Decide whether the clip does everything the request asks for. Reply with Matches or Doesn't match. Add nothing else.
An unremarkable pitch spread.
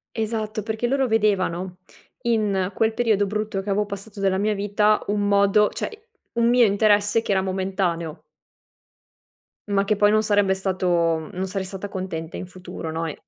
Doesn't match